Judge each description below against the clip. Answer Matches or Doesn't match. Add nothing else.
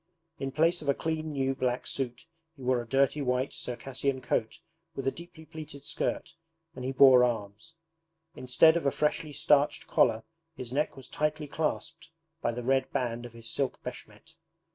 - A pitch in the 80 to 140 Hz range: Matches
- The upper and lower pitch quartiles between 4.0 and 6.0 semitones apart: Doesn't match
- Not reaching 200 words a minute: Matches